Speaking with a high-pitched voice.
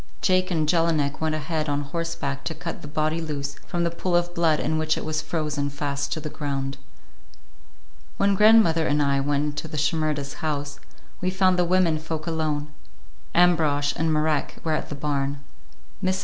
No: medium, 155 Hz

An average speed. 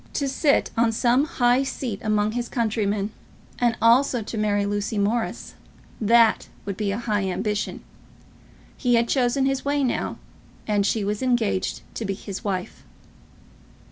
Yes: average, 150 wpm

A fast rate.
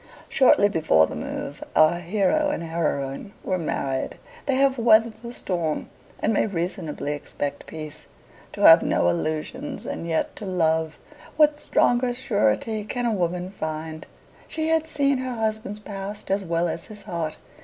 No: average, 155 wpm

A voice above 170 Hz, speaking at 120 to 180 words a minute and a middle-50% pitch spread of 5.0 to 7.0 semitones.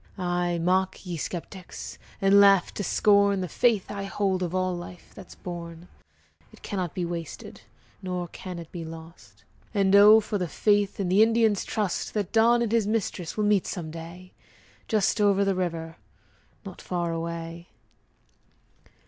No: medium, 185 Hz; average, 160 wpm; average, 2.8 semitones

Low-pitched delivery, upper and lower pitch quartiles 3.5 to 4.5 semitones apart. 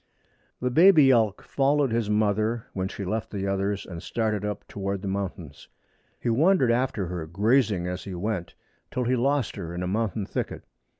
Yes: low, 105 Hz; average, 3.9 semitones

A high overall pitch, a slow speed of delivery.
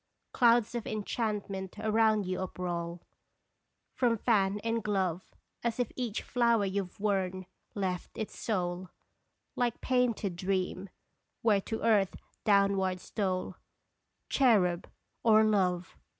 Yes: high, 200 Hz; slow, 115 wpm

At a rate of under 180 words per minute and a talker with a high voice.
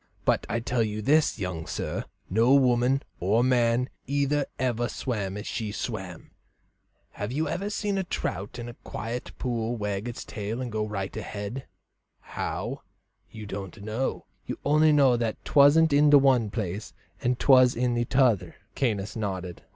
No: average, 160 wpm; low, 120 Hz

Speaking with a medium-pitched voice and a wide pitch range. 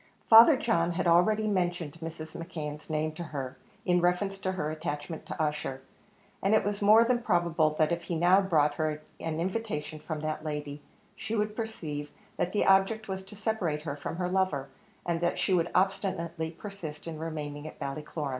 No: medium, 170 Hz; average, 3.9 semitones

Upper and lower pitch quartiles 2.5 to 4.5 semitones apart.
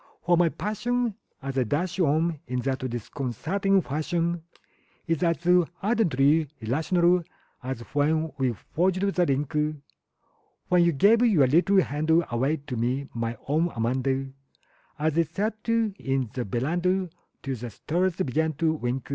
No: average, 5.2 semitones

